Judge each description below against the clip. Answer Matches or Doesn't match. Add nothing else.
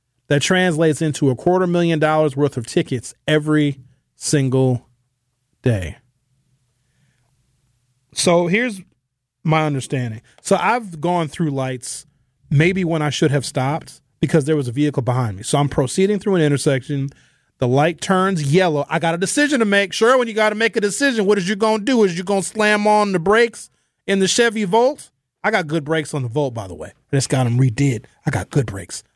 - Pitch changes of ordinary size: Doesn't match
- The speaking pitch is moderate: Matches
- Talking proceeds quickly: Doesn't match